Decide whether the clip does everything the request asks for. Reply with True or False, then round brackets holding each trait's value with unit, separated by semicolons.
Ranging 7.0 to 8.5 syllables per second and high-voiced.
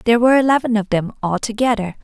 True (7.3 syllables/s; 225 Hz)